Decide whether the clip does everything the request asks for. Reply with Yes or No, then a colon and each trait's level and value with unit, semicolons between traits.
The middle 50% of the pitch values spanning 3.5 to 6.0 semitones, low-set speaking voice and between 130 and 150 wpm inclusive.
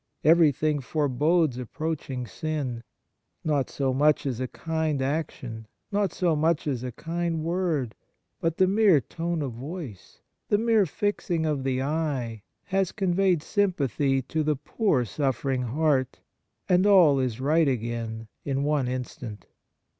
No: average, 4.4 semitones; medium, 150 Hz; average, 140 wpm